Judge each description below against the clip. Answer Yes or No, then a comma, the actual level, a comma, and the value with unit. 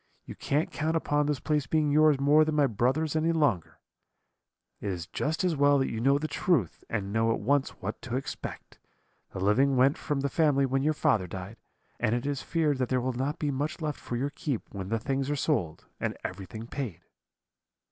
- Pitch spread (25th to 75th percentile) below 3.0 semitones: No, average, 4.3 semitones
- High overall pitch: No, medium, 140 Hz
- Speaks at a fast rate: Yes, fast, 210 wpm